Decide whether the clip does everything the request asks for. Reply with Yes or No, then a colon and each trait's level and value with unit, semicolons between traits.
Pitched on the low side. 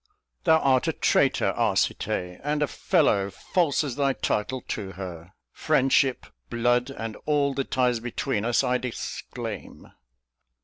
Yes: low, 125 Hz